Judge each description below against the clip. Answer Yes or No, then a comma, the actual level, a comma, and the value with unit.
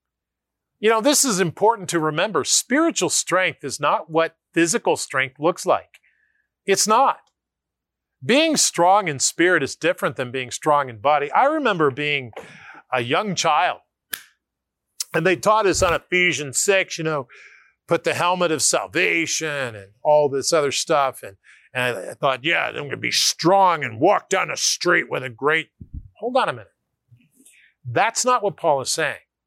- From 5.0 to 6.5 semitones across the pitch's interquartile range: Yes, average, 5.3 semitones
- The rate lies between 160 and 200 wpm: Yes, average, 165 wpm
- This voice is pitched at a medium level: Yes, medium, 165 Hz